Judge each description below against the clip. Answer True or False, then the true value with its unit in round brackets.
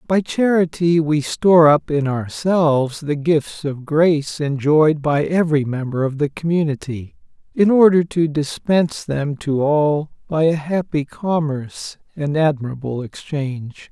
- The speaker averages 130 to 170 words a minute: True (140 wpm)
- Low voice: False (150 Hz)